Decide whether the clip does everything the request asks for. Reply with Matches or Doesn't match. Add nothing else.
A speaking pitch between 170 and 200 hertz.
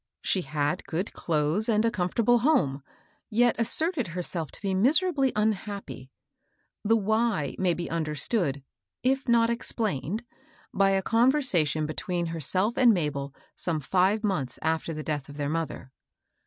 Matches